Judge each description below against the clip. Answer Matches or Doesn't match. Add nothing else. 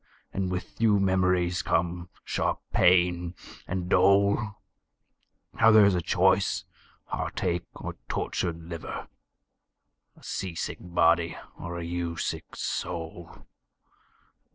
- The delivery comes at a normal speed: Doesn't match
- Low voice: Matches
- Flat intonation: Matches